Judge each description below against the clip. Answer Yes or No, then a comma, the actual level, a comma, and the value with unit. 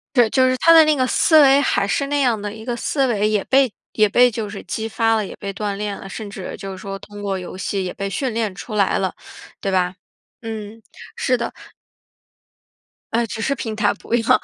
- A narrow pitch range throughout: No, average, 3.7 semitones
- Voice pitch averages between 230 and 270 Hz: No, high, 220 Hz